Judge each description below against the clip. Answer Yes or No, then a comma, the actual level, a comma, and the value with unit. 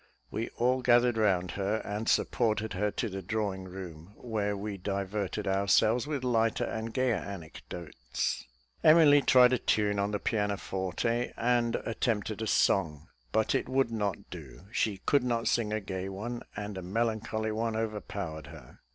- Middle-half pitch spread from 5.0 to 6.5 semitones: No, average, 3.2 semitones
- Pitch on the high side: No, low, 105 Hz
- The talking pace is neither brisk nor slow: Yes, average, 160 wpm